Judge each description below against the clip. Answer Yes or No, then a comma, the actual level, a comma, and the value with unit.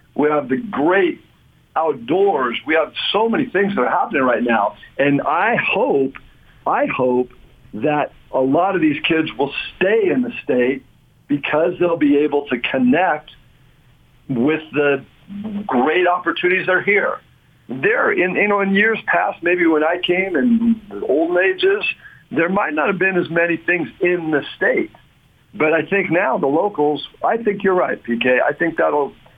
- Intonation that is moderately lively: No, wide, 6.0 semitones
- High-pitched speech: No, medium, 165 Hz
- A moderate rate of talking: Yes, average, 170 wpm